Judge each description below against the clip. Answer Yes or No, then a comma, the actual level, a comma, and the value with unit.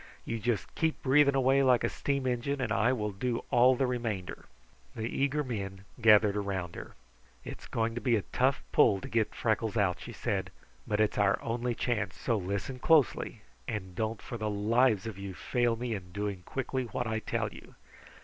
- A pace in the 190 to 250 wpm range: Yes, average, 195 wpm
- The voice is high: No, low, 115 Hz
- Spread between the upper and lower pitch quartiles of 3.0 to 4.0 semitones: Yes, average, 3.6 semitones